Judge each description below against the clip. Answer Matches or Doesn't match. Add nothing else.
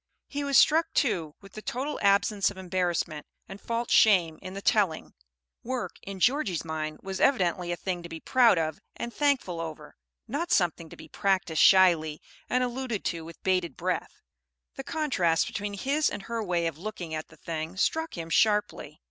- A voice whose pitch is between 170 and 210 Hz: Matches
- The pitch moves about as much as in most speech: Doesn't match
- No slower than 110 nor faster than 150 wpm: Doesn't match